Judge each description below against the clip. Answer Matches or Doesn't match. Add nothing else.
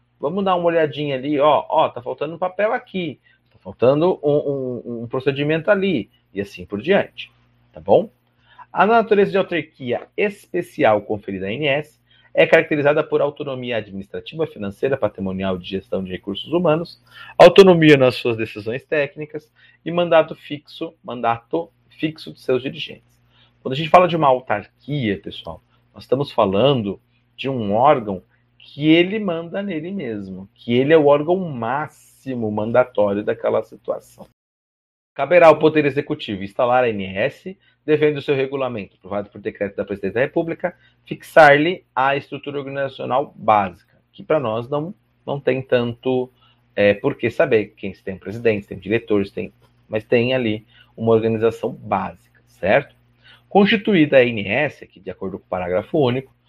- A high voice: Doesn't match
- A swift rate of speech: Doesn't match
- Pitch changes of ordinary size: Doesn't match